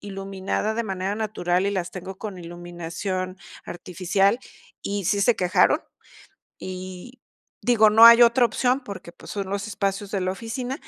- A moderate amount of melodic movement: Yes, average, 3.0 semitones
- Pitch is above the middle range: Yes, high, 195 Hz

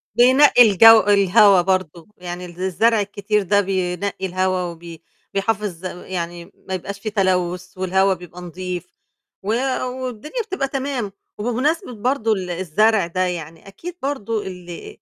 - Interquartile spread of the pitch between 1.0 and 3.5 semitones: No, average, 3.9 semitones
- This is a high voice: Yes, high, 195 Hz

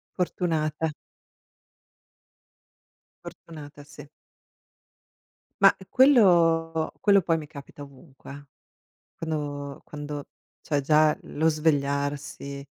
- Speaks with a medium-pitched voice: Yes, medium, 150 Hz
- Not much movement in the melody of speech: Yes, narrow, 2.3 semitones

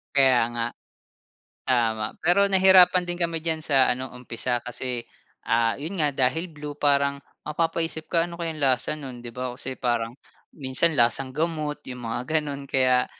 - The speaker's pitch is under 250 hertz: Yes, medium, 140 Hz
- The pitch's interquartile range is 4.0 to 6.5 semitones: Yes, average, 4.4 semitones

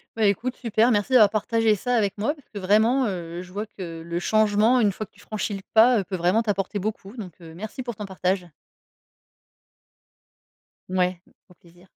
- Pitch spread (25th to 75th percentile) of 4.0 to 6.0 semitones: No, average, 3.2 semitones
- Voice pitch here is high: Yes, high, 205 Hz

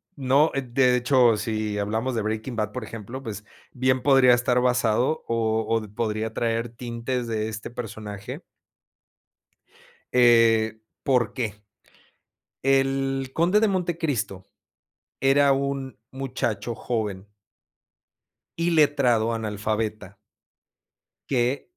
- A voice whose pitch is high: No, low, 120 Hz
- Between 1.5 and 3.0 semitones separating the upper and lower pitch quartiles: No, average, 3.4 semitones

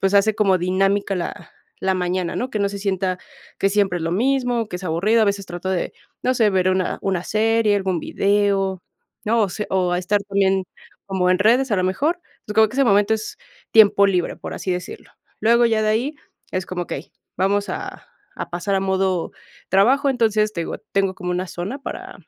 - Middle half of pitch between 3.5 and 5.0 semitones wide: No, average, 2.7 semitones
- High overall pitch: Yes, high, 195 Hz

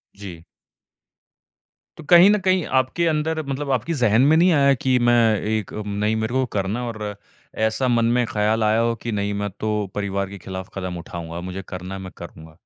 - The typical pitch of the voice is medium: No, low, 110 Hz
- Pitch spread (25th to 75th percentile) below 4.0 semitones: No, average, 5.2 semitones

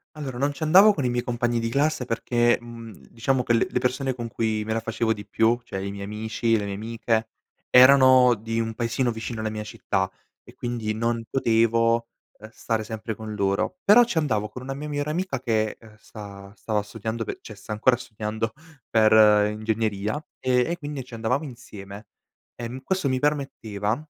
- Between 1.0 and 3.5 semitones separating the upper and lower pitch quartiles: Yes, average, 2.9 semitones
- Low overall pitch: Yes, low, 115 Hz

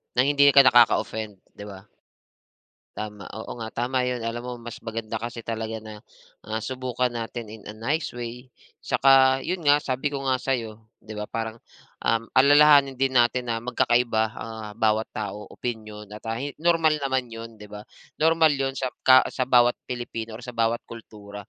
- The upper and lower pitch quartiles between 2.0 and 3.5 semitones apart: Yes, average, 2.9 semitones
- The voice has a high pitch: No, low, 120 Hz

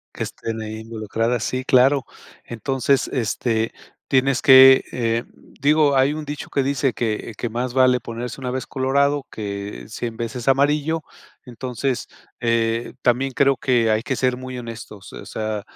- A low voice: Yes, low, 125 Hz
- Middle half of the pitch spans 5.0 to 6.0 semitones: No, average, 2.9 semitones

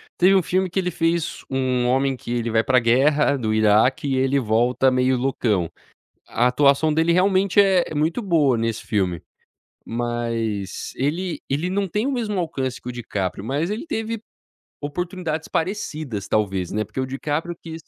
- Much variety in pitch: Yes, wide, 6.4 semitones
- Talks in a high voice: No, low, 135 Hz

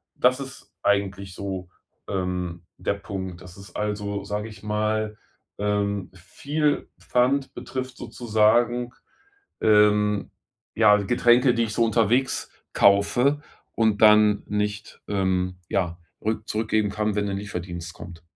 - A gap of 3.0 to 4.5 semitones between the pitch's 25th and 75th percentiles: No, narrow, 2.4 semitones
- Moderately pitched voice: No, low, 105 Hz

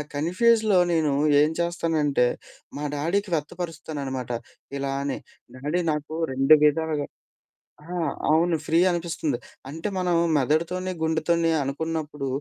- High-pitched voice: No, medium, 160 Hz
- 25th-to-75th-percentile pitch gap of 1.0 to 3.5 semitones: Yes, average, 2.8 semitones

